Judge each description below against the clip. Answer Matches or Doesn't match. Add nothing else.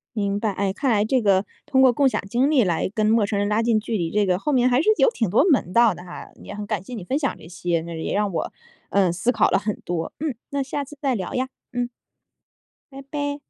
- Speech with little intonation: Doesn't match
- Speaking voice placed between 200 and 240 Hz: Matches